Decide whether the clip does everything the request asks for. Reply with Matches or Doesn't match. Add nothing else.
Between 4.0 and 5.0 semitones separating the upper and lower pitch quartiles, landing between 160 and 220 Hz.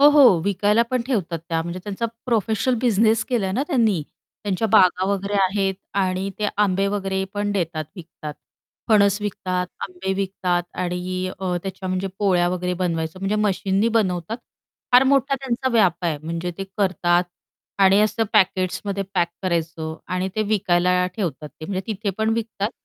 Doesn't match